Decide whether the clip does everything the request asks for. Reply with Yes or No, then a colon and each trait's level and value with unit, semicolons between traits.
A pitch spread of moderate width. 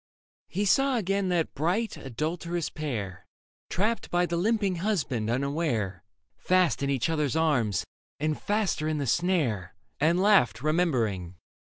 No: wide, 6.6 semitones